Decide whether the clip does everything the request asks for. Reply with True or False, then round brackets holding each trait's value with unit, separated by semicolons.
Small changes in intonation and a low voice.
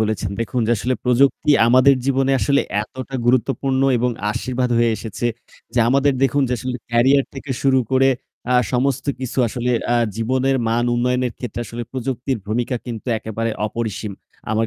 True (2.3 semitones; 125 Hz)